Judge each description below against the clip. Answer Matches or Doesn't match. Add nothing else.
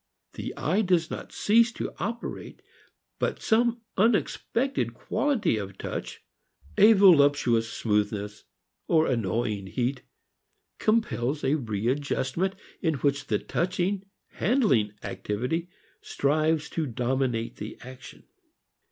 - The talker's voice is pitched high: Doesn't match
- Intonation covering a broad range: Matches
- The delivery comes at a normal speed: Doesn't match